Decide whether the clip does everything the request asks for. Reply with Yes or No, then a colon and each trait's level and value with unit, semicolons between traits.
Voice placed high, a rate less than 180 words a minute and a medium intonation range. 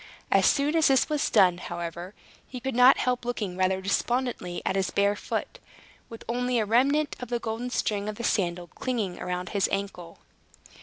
No: high, 220 Hz; average, 185 wpm; average, 4.9 semitones